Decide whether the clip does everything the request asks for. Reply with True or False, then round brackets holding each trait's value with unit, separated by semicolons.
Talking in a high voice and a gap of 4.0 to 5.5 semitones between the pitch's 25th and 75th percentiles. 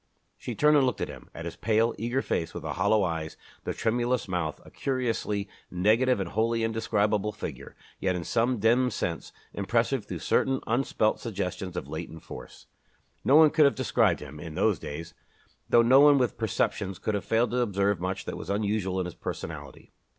False (110 Hz; 4.6 semitones)